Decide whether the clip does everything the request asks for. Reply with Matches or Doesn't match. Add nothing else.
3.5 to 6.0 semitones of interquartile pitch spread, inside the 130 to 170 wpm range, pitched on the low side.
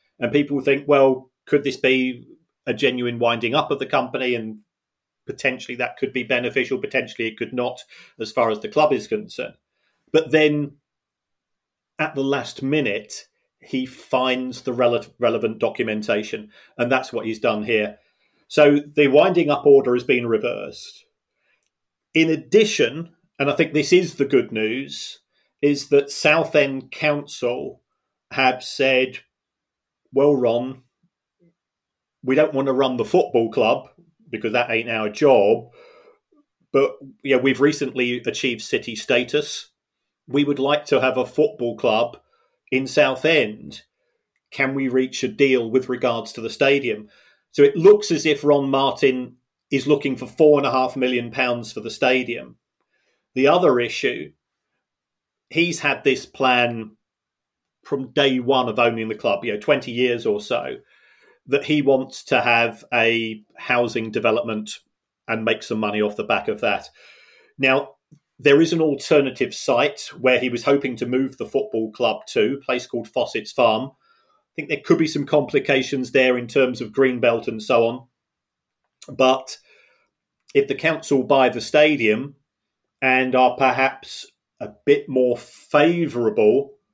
Doesn't match